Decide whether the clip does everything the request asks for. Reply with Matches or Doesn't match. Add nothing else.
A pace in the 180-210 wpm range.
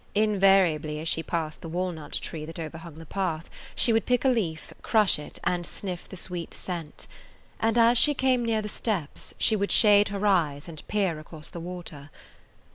Matches